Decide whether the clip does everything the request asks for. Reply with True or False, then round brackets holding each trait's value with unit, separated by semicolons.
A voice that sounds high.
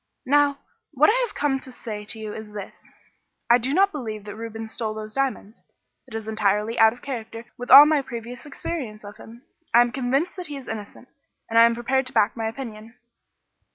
True (235 Hz)